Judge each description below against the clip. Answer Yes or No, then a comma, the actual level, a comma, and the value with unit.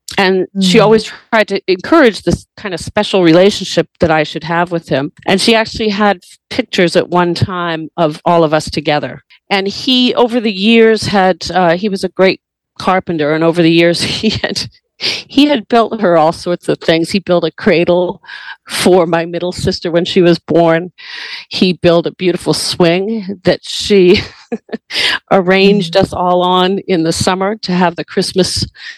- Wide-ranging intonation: No, average, 3.2 semitones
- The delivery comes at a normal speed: Yes, average, 180 wpm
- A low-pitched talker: No, medium, 185 Hz